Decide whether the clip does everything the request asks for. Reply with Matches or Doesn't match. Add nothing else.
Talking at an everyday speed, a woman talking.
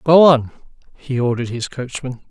Doesn't match